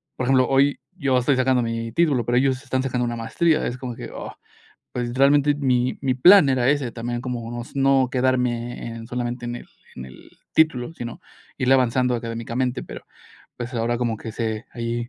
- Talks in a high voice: No, low, 125 Hz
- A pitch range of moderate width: No, narrow, 2.0 semitones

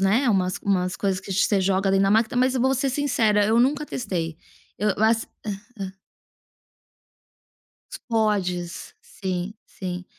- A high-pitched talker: Yes, high, 200 Hz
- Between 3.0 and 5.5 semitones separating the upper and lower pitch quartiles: Yes, average, 3.6 semitones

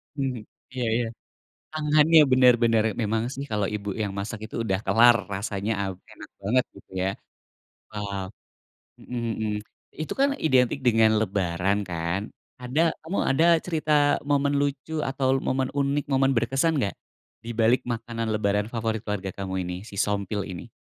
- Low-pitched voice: Yes, low, 115 Hz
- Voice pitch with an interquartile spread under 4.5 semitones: No, average, 4.8 semitones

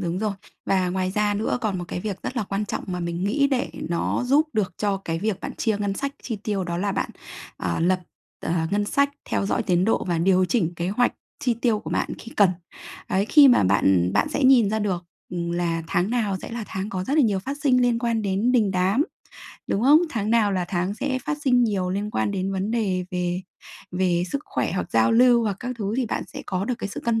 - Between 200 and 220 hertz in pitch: Yes, high, 205 Hz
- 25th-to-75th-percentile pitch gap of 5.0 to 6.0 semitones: No, average, 4.3 semitones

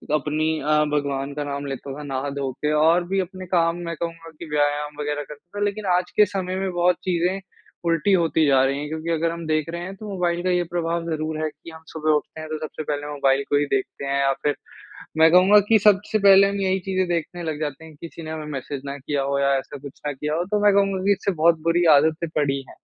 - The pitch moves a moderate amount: Yes, average, 3.5 semitones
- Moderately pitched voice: Yes, medium, 160 Hz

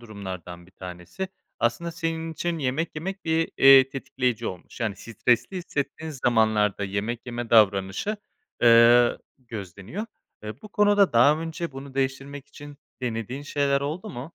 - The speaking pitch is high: No, low, 130 Hz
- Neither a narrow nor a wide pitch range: No, wide, 6.4 semitones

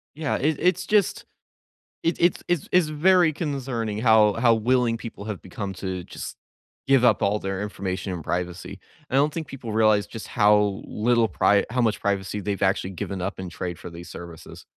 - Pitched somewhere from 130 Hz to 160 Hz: No, low, 105 Hz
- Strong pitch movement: Yes, wide, 5.8 semitones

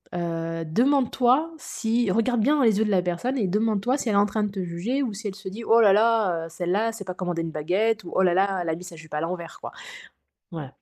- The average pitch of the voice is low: No, high, 200 Hz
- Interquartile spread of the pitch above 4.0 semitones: Yes, average, 4.6 semitones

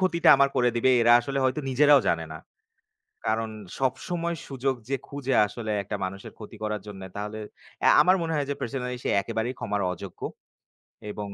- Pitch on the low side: Yes, low, 125 Hz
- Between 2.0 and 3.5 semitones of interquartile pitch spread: No, average, 4.7 semitones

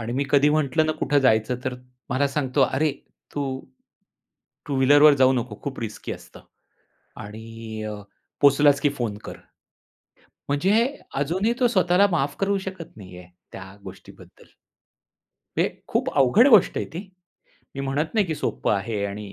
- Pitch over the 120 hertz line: Yes, medium, 140 Hz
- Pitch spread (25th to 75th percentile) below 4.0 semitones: No, wide, 5.5 semitones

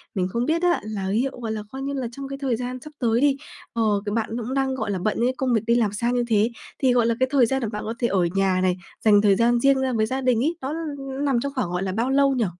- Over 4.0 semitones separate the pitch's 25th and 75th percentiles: No, average, 3.7 semitones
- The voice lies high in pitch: Yes, high, 240 Hz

